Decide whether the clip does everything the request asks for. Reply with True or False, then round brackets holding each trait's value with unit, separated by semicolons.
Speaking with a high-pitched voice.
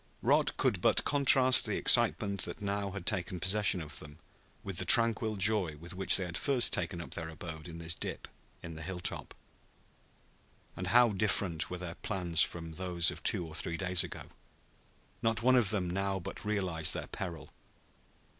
False (90 Hz)